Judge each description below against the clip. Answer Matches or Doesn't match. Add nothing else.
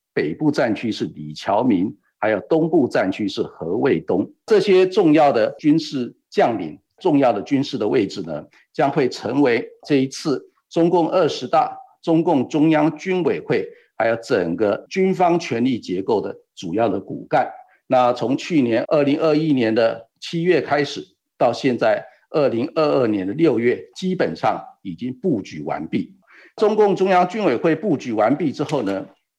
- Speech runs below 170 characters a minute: Doesn't match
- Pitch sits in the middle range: Matches